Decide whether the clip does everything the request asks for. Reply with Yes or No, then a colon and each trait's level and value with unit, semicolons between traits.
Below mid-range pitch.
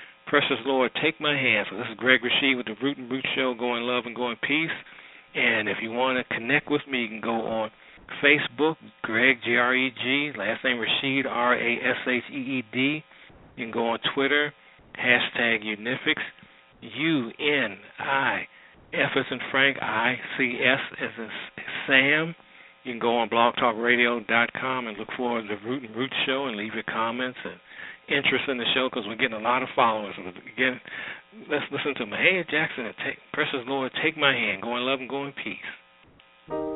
Yes: low, 125 Hz